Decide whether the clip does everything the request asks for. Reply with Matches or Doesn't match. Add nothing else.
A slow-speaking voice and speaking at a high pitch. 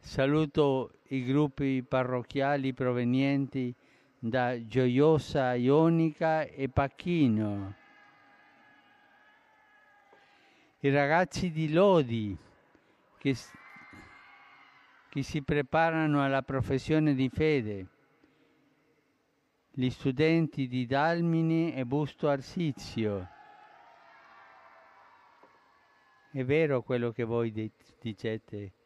Doesn't match